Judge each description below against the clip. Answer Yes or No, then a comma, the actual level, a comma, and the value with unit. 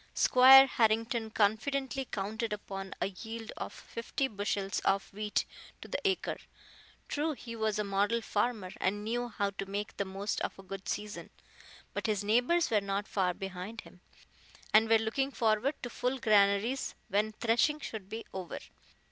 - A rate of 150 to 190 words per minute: Yes, average, 165 wpm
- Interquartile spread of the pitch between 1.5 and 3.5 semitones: Yes, average, 3.0 semitones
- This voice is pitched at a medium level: No, high, 215 Hz